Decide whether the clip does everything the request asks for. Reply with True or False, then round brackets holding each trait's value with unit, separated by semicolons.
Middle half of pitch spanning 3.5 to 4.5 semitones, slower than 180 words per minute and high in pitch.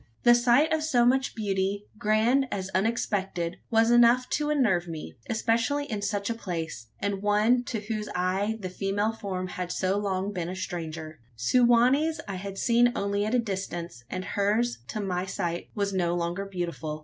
False (4.2 semitones; 185 wpm; 200 Hz)